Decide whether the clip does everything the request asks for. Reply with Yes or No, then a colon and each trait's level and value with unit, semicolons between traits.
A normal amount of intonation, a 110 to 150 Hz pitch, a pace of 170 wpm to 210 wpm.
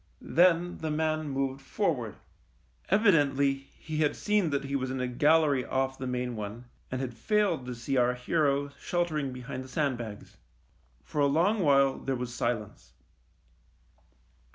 No: average, 3.7 semitones; low, 135 Hz; average, 155 wpm